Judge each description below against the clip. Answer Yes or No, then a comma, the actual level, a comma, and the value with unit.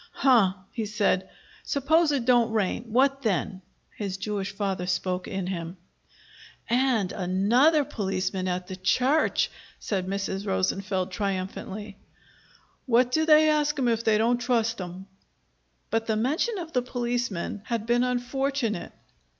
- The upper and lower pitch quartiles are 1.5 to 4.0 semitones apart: No, average, 4.7 semitones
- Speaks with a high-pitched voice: Yes, high, 220 Hz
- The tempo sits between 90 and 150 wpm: Yes, slow, 135 wpm